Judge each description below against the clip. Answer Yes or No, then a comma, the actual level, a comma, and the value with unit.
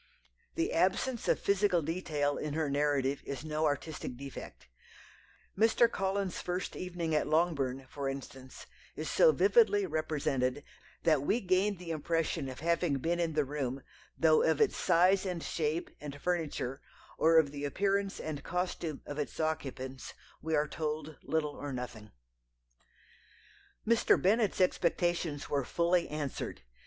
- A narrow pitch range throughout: No, average, 3.8 semitones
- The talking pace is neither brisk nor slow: Yes, average, 145 wpm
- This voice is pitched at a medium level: Yes, medium, 155 Hz